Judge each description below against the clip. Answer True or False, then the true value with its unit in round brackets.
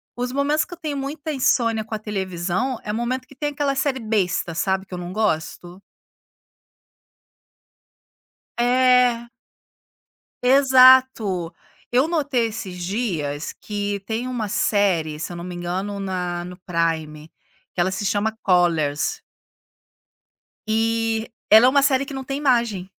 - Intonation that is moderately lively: False (6.1 semitones)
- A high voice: True (220 Hz)